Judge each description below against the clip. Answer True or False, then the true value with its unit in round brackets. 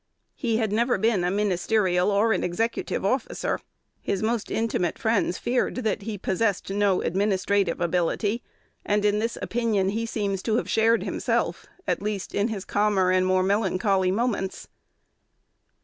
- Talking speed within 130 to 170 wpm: True (150 wpm)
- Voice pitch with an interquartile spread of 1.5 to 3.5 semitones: True (2.9 semitones)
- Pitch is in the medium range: False (205 Hz)